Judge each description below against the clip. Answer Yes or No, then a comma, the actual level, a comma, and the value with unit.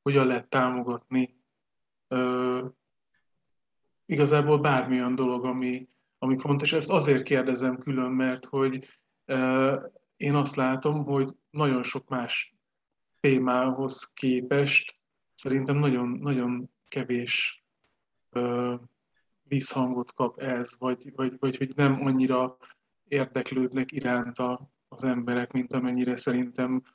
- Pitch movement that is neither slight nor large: No, narrow, 1.5 semitones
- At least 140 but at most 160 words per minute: No, slow, 105 wpm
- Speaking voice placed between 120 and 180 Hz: Yes, low, 130 Hz